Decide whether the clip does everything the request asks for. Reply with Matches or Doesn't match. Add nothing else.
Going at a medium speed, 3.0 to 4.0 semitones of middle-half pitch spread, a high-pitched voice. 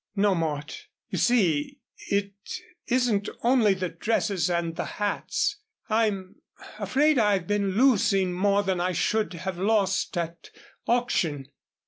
Doesn't match